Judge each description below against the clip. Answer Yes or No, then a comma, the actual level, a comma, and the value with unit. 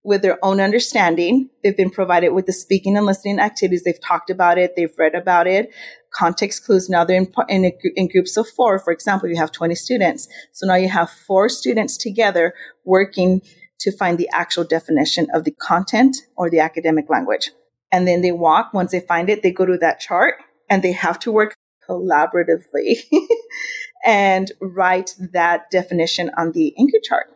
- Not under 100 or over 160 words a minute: No, average, 185 wpm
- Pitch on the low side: No, medium, 185 Hz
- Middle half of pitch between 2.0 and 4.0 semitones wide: Yes, average, 2.8 semitones